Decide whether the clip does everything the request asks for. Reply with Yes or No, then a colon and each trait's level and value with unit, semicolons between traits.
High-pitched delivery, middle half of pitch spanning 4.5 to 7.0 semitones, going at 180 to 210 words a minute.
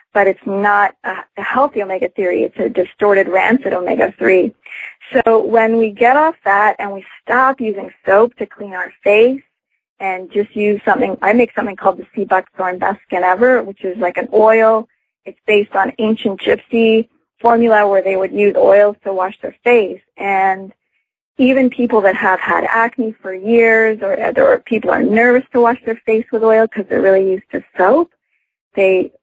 No: high, 215 Hz; average, 3.2 semitones; average, 185 wpm